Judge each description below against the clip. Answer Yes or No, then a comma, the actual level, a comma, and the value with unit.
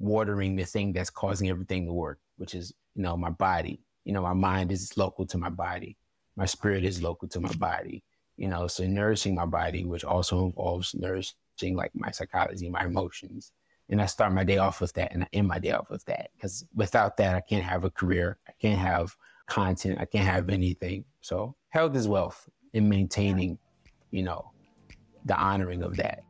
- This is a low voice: Yes, very low, 95 Hz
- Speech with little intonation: Yes, narrow, 1.7 semitones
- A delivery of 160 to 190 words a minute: No, fast, 205 wpm